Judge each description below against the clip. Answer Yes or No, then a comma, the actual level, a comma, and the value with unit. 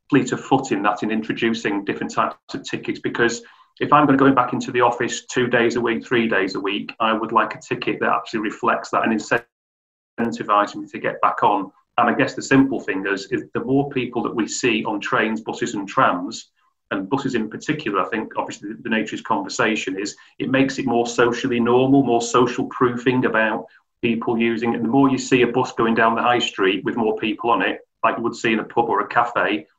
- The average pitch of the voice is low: Yes, low, 120 Hz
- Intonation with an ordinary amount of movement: No, narrow, 1.8 semitones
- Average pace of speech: No, fast, 230 wpm